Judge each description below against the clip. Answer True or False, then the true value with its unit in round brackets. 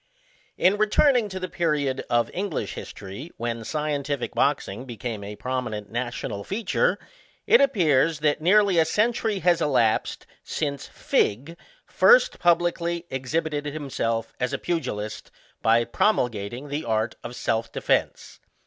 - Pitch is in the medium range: True (145 Hz)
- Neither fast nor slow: False (130 wpm)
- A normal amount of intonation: False (6.5 semitones)